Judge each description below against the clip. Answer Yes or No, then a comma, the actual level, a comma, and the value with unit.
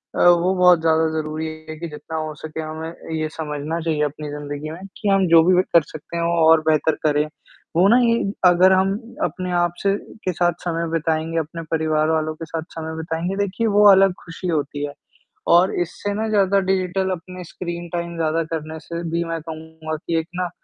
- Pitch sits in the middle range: Yes, medium, 165 Hz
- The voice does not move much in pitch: Yes, narrow, 2.3 semitones